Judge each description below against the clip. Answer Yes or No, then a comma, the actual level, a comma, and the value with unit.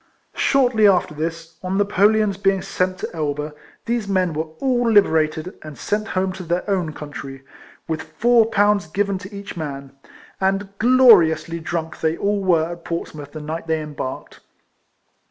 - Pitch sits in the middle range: Yes, medium, 180 Hz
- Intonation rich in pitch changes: No, average, 4.3 semitones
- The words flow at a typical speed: Yes, average, 160 wpm